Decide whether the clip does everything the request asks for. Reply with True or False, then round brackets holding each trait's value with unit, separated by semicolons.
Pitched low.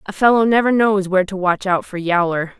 False (195 Hz)